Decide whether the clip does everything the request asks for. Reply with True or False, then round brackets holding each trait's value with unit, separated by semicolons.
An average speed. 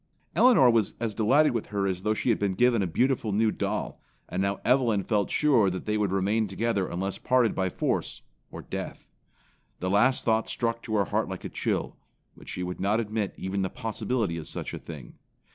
False (210 wpm)